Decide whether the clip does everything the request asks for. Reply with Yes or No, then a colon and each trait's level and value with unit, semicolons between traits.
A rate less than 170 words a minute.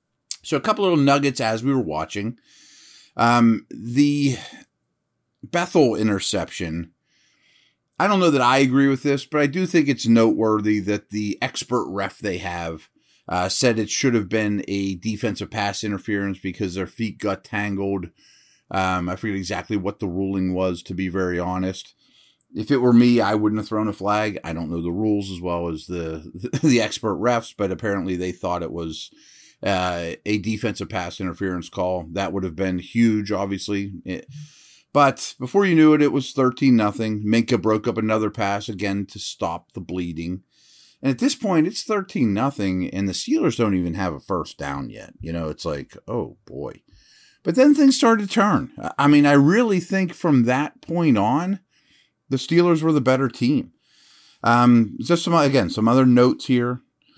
No: average, 180 wpm